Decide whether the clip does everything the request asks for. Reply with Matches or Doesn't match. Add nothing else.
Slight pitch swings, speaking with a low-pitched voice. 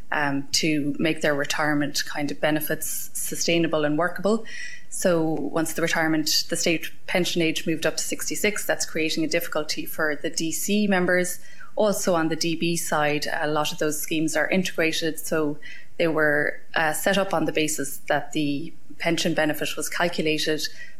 Doesn't match